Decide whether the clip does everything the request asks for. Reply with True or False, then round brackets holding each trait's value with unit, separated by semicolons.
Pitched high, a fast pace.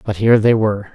False (105 Hz; 255 wpm)